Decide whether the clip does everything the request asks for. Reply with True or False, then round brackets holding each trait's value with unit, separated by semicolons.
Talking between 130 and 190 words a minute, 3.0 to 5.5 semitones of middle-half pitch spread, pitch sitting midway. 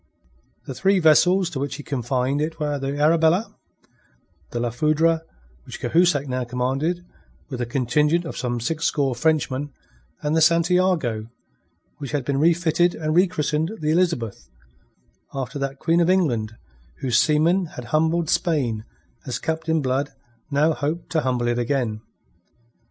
True (145 wpm; 4.2 semitones; 150 Hz)